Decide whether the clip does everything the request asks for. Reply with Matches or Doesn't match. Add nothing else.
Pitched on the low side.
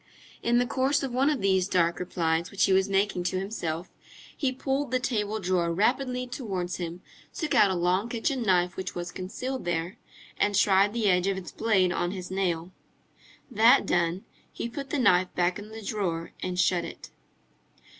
Doesn't match